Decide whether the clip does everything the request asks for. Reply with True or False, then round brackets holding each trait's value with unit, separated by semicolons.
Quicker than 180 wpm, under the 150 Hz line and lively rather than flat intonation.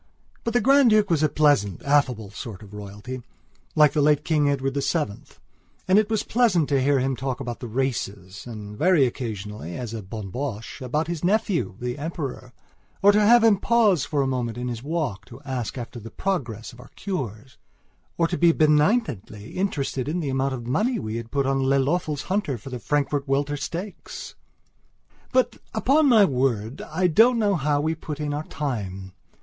True (190 wpm; 140 Hz; 6.1 semitones)